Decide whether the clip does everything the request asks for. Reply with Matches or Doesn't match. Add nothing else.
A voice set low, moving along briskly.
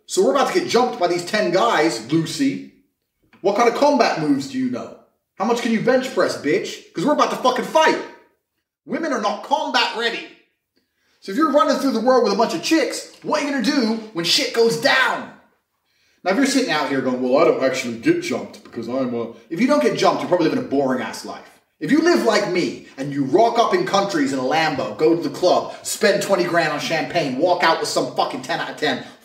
Doesn't match